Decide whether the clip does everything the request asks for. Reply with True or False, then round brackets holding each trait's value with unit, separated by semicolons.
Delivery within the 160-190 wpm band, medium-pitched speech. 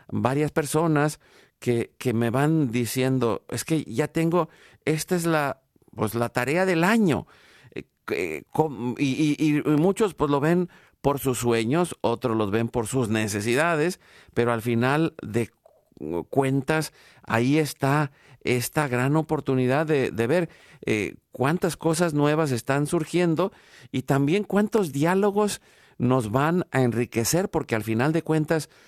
False (145 wpm; 145 Hz)